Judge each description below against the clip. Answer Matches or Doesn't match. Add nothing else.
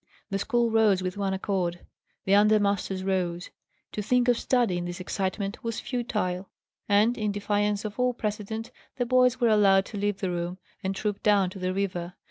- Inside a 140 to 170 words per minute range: Doesn't match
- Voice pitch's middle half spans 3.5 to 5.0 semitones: Doesn't match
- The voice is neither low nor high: Doesn't match